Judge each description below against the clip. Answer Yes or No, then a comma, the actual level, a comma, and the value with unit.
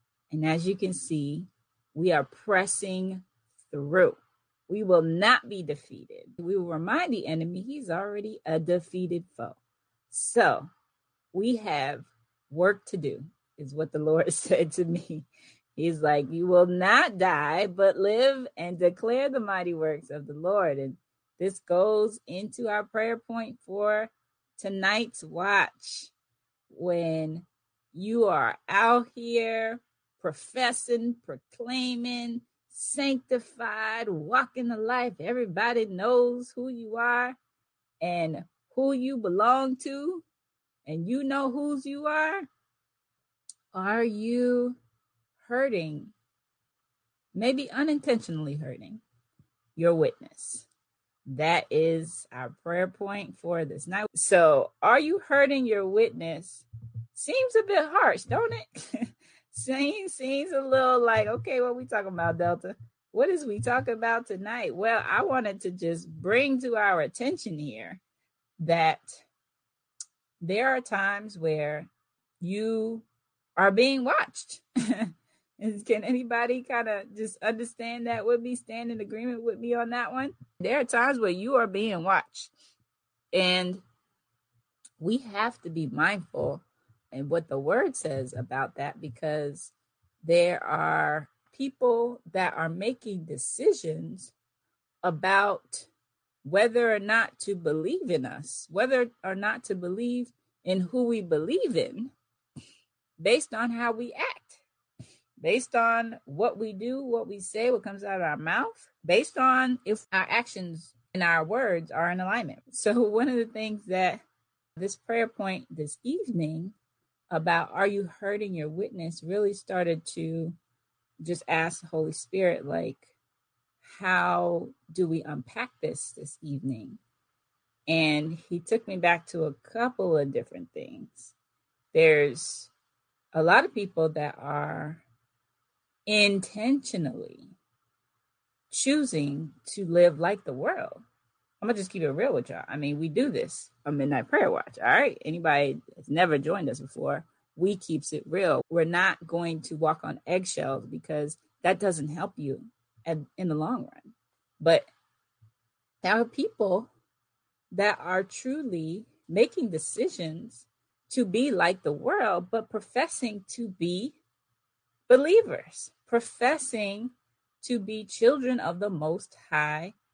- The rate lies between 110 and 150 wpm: Yes, slow, 135 wpm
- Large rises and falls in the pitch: Yes, wide, 6.6 semitones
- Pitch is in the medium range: No, high, 195 Hz